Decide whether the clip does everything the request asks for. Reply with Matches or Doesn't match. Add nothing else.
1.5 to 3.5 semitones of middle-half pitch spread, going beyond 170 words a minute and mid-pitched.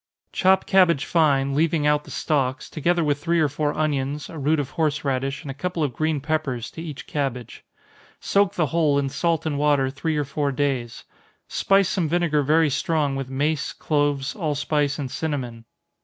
Matches